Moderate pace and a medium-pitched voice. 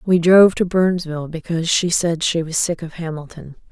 Yes: average, 195 wpm; medium, 170 Hz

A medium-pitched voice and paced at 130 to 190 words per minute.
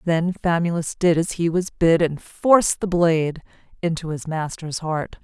Yes: medium, 170 Hz; average, 170 wpm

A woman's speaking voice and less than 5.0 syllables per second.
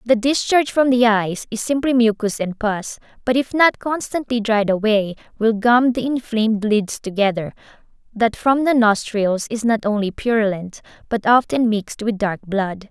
Yes: female; 4.7 syllables/s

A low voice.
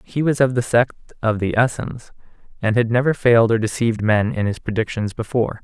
Yes: low, 115 Hz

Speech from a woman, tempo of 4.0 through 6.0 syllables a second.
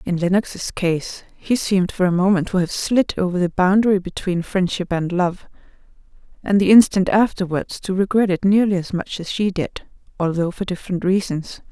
Yes: female; 5.1 syllables/s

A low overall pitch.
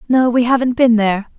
No: high, 240 Hz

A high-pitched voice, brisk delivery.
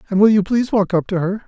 Yes: high, 200 Hz; fast, 325 wpm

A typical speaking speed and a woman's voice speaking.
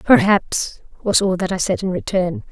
Yes: average, 190 wpm; female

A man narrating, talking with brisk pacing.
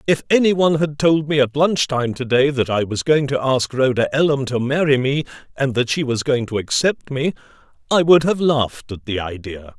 Yes: male; fast, 225 wpm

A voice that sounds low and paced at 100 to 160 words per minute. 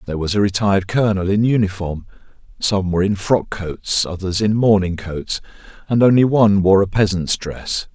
No: low, 100 Hz; average, 175 wpm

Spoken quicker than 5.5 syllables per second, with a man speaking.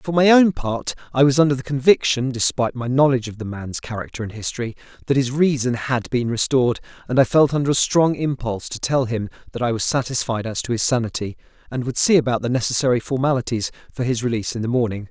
Yes: 6.4 syllables/s; male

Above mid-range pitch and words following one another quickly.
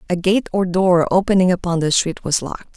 No: medium, 175 Hz; fast, 215 wpm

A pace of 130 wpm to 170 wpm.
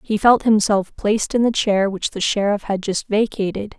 No: fast, 205 wpm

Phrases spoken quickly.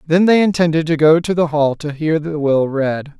Yes: fast, 245 wpm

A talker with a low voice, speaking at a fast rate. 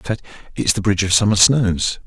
Yes: low, 105 Hz; fast, 230 wpm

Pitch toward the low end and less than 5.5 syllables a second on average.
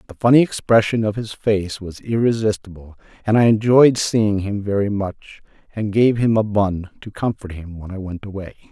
Yes: low, 105 Hz; 5.0 syllables/s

